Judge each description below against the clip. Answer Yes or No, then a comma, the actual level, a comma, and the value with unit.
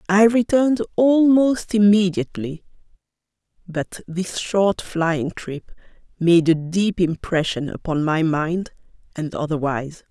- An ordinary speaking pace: No, slow, 105 wpm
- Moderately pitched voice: Yes, medium, 180 Hz